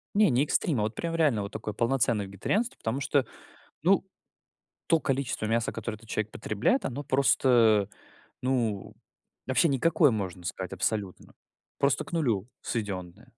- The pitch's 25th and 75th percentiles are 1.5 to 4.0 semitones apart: No, average, 4.8 semitones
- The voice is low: Yes, low, 120 Hz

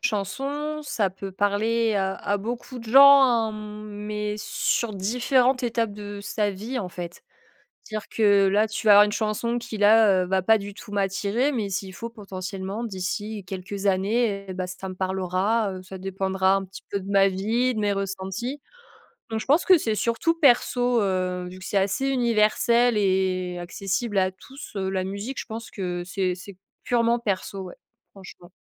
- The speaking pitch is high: Yes, high, 205 Hz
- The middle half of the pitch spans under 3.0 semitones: No, average, 3.3 semitones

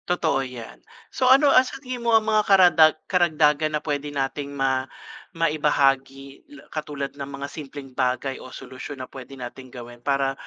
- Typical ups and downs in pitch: Yes, average, 3.0 semitones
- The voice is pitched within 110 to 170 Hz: Yes, medium, 140 Hz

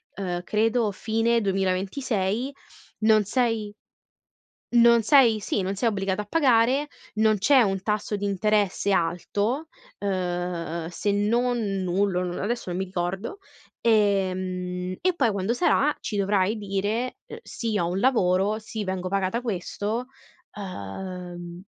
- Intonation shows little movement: No, average, 3.5 semitones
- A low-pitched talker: No, high, 205 Hz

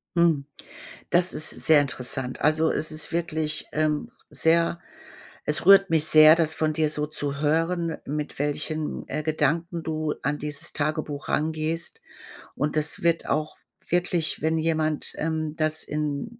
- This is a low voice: No, medium, 155 Hz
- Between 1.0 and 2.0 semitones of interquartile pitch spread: Yes, narrow, 1.4 semitones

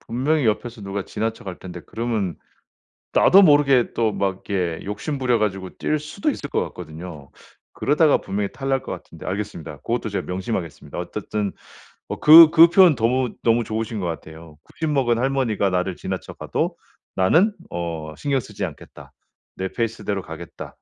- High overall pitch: No, low, 110 Hz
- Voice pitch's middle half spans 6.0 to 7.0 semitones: Yes, wide, 6.4 semitones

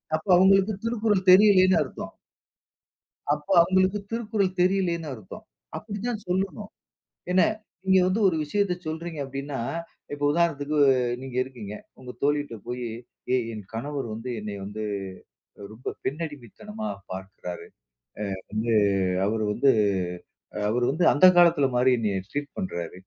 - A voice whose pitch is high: No, medium, 150 Hz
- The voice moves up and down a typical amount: No, wide, 7.3 semitones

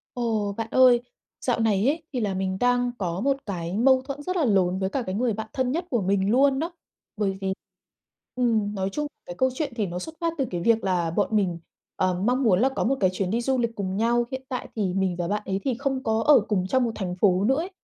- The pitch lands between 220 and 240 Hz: Yes, high, 225 Hz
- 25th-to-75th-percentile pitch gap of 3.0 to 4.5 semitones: No, average, 5.2 semitones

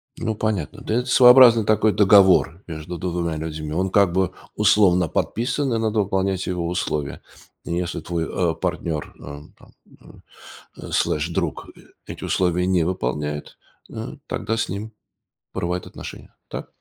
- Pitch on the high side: No, very low, 90 Hz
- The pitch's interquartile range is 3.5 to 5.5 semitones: Yes, average, 4.0 semitones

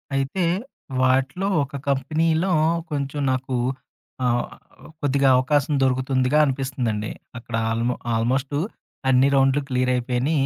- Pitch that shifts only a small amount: Yes, narrow, 2.0 semitones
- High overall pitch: No, low, 135 Hz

